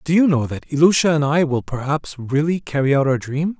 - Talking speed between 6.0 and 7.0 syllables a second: No, 5.6 syllables/s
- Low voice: No, medium, 150 Hz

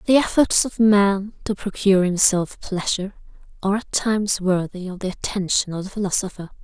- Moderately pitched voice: No, high, 195 Hz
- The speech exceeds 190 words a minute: No, average, 165 wpm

